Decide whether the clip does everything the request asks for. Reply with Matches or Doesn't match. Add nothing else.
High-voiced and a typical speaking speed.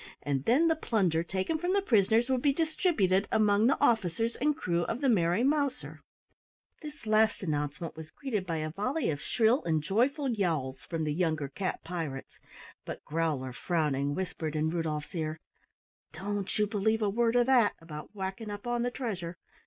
Matches